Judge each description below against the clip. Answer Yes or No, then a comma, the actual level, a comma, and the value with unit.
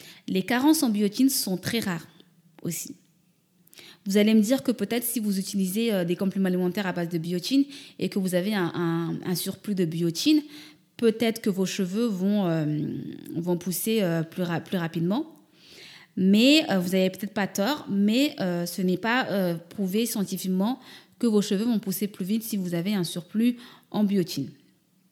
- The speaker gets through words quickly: No, average, 180 wpm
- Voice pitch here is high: Yes, high, 195 Hz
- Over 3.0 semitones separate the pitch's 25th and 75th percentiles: Yes, average, 4.0 semitones